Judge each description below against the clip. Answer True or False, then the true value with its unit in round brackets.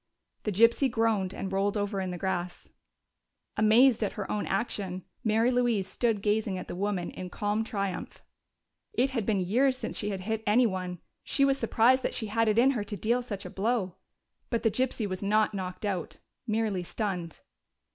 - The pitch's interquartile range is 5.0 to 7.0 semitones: False (3.1 semitones)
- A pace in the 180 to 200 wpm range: True (185 wpm)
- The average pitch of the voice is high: True (210 Hz)